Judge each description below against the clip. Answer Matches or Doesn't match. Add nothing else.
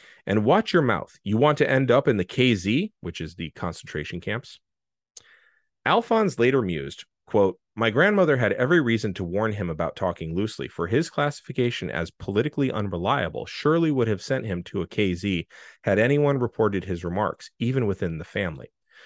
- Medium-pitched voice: Doesn't match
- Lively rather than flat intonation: Matches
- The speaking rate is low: Doesn't match